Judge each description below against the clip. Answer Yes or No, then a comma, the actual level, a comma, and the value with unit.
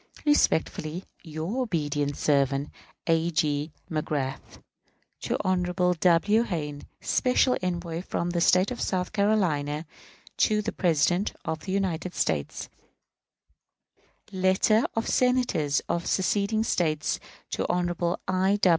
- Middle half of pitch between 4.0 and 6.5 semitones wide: Yes, average, 4.4 semitones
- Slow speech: Yes, slow, 110 wpm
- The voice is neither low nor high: Yes, medium, 175 Hz